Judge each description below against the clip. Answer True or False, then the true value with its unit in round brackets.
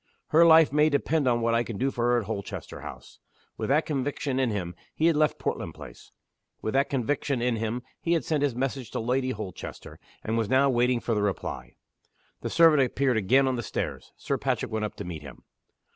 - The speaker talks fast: True (220 wpm)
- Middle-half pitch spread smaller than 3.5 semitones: False (4.0 semitones)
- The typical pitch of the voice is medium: False (125 Hz)